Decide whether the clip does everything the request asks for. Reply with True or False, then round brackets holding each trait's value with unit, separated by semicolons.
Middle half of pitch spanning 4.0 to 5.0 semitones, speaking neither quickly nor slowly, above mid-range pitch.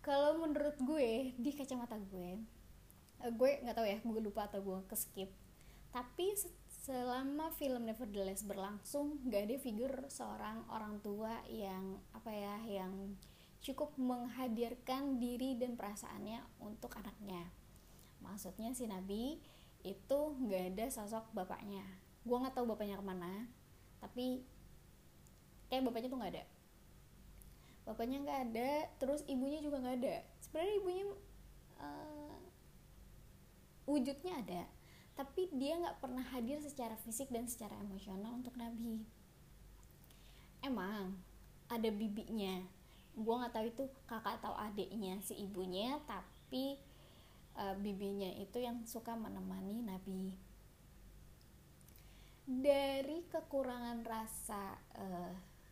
True (4.6 semitones; 115 wpm; 235 Hz)